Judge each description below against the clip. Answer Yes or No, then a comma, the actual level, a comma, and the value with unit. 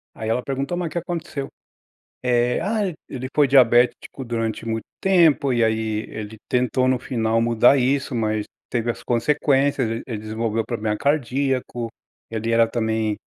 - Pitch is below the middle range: Yes, low, 120 Hz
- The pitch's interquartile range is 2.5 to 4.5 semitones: Yes, average, 3.4 semitones